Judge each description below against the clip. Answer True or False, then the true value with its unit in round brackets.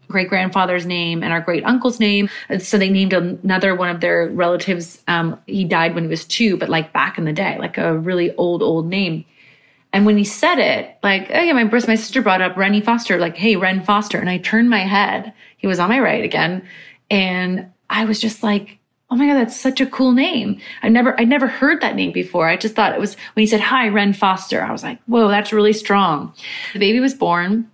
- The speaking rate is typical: False (240 wpm)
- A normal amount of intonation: True (3.9 semitones)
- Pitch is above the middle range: True (200 Hz)